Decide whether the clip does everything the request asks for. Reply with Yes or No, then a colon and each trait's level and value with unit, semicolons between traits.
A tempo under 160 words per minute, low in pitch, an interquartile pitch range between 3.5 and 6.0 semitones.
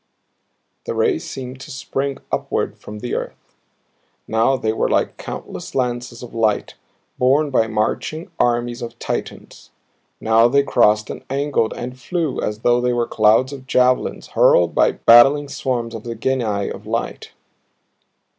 No: average, 150 wpm; low, 120 Hz; average, 2.9 semitones